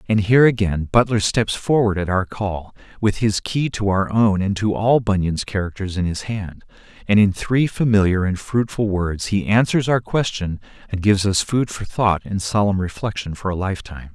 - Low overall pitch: Yes, low, 100 Hz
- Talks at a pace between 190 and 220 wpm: Yes, average, 195 wpm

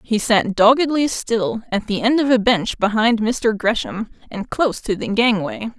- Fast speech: No, average, 185 wpm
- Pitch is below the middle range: No, high, 220 Hz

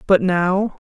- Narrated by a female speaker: Yes, female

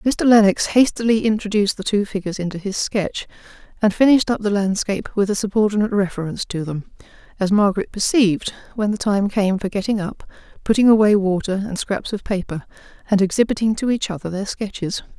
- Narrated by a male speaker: No, female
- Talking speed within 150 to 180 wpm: Yes, average, 175 wpm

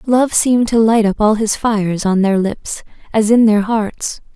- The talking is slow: No, fast, 205 wpm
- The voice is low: No, high, 215 Hz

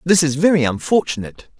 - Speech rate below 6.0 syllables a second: No, 6.3 syllables/s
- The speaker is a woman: No, male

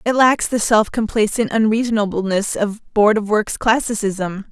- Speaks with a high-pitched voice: Yes, high, 215 Hz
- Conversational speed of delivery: Yes, average, 145 wpm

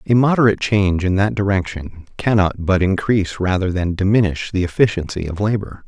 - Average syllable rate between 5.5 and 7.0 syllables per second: Yes, 5.7 syllables/s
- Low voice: Yes, very low, 95 Hz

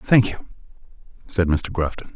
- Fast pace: No, average, 140 wpm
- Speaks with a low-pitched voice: Yes, very low, 90 Hz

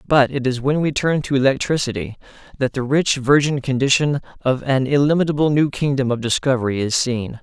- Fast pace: No, average, 180 wpm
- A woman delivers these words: No, male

